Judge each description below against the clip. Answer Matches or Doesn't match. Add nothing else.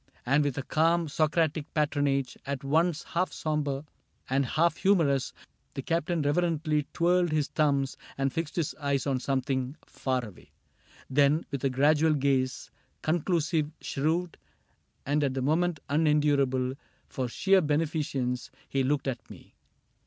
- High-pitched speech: Doesn't match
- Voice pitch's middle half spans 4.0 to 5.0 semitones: Doesn't match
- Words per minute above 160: Doesn't match